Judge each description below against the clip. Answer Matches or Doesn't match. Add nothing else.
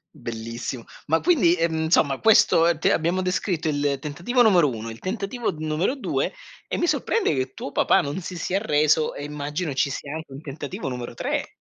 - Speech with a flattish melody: Doesn't match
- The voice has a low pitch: Doesn't match